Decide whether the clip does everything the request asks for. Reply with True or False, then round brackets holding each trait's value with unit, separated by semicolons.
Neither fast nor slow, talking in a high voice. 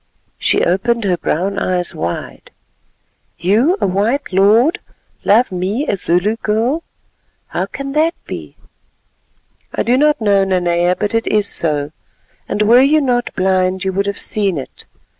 True (150 wpm; 200 Hz)